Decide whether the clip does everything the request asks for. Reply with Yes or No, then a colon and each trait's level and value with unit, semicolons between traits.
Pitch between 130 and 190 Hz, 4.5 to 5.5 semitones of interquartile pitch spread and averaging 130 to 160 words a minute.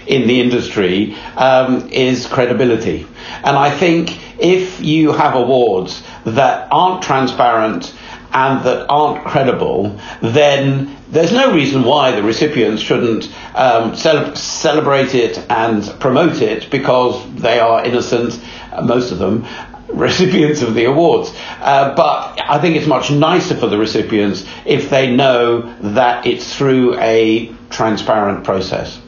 No: low, 135 Hz; average, 4.1 semitones; slow, 135 wpm